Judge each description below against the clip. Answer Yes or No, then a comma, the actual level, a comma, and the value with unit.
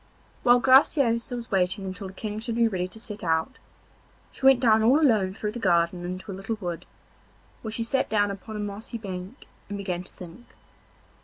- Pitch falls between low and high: No, high, 210 Hz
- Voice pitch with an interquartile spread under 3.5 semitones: No, average, 3.8 semitones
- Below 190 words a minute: No, average, 200 wpm